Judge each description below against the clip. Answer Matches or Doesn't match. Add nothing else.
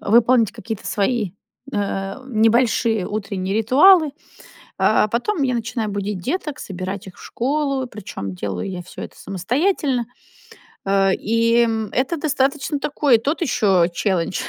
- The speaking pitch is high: Matches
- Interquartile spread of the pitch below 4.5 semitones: Doesn't match